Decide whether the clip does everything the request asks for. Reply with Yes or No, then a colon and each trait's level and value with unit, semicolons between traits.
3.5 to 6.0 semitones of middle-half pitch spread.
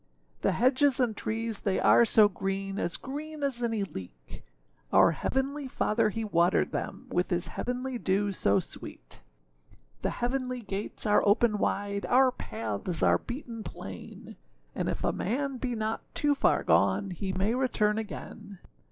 Yes: average, 4.6 semitones